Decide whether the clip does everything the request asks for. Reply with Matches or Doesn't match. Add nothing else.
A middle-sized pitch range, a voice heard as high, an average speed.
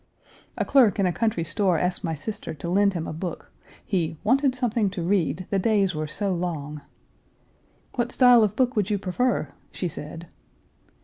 Matches